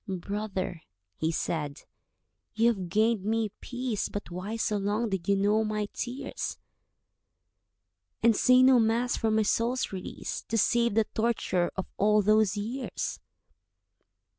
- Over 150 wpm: No, average, 140 wpm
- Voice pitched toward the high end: Yes, high, 215 Hz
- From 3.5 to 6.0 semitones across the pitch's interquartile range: No, average, 2.8 semitones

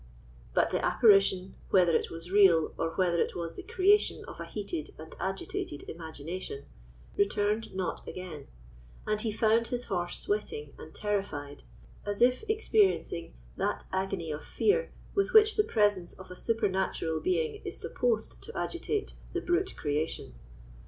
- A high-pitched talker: Yes, high, 195 Hz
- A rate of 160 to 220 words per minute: No, average, 150 wpm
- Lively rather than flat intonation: Yes, wide, 6.3 semitones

